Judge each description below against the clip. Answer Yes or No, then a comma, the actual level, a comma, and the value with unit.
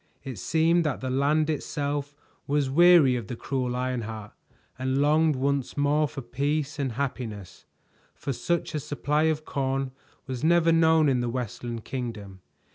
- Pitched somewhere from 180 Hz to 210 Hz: No, medium, 140 Hz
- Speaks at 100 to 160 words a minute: Yes, average, 155 wpm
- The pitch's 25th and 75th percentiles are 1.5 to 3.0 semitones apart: No, average, 3.4 semitones